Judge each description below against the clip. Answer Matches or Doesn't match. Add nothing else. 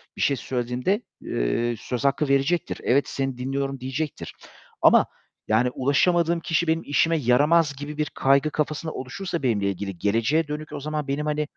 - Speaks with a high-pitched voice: Doesn't match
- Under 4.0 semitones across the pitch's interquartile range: Matches